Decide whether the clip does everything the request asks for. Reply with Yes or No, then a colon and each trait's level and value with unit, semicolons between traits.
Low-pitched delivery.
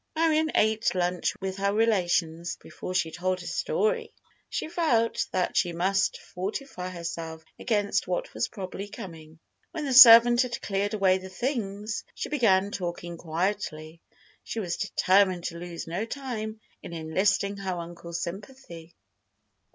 No: high, 190 Hz